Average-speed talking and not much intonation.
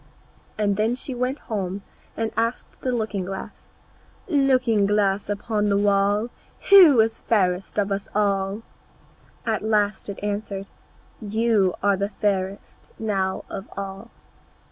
No: slow, 130 wpm; narrow, 2.3 semitones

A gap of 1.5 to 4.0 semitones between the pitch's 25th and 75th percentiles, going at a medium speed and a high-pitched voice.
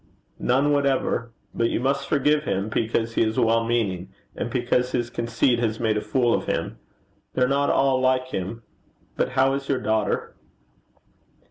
No: average, 2.9 semitones; average, 165 wpm; low, 120 Hz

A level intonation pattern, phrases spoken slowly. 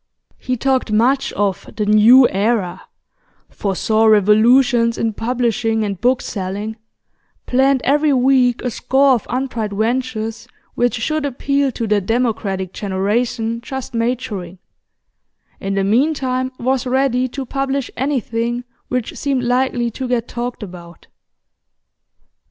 No: average, 3.2 semitones; slow, 125 wpm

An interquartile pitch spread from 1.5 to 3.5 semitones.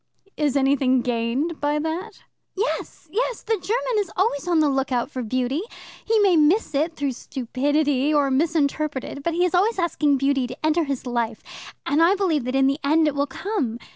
No: average, 4.3 semitones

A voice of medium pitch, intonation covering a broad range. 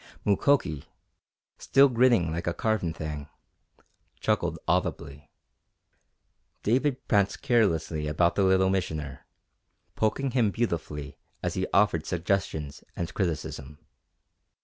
No: very low, 90 Hz; wide, 6.1 semitones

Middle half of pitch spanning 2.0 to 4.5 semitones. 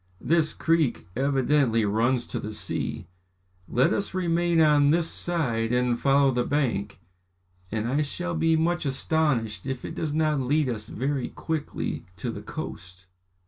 No: average, 5.0 semitones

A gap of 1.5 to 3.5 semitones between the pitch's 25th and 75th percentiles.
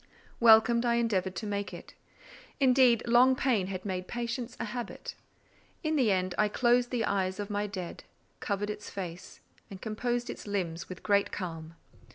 No: average, 4.1 semitones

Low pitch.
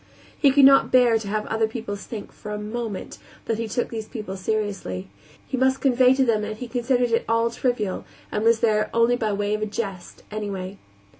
No: high, 220 Hz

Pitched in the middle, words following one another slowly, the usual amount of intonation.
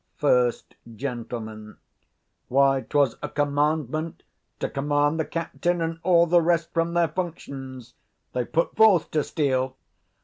Yes: medium, 150 Hz; slow, 130 wpm; average, 3.6 semitones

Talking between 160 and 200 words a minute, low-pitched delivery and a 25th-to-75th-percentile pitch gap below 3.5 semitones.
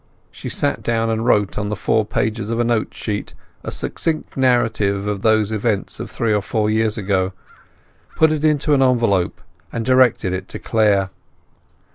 Yes: average, 175 wpm; low, 110 Hz; narrow, 2.6 semitones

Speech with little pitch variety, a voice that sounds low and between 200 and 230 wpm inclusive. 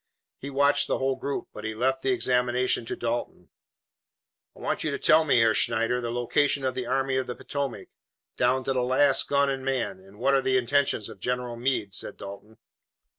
Yes: narrow, 2.3 semitones; low, 125 Hz; fast, 205 wpm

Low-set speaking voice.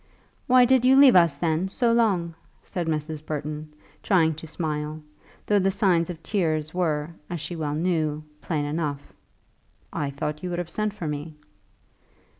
No: medium, 160 Hz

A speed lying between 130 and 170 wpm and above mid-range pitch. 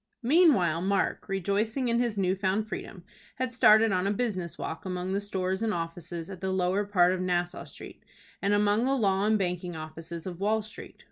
No: average, 195 wpm; high, 195 Hz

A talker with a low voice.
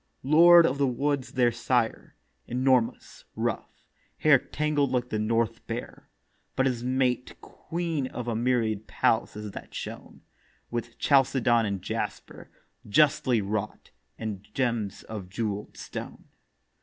Yes: low, 120 Hz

